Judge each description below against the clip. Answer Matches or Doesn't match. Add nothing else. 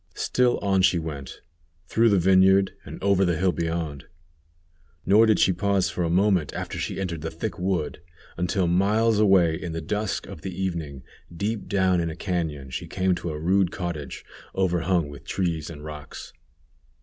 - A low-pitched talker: Matches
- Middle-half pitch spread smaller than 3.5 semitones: Matches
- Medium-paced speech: Matches